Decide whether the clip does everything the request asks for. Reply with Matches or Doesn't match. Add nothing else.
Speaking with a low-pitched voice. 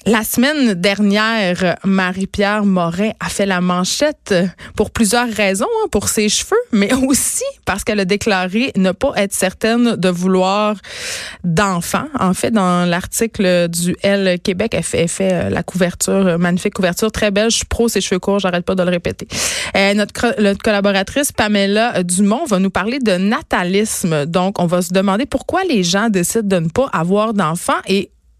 Doesn't match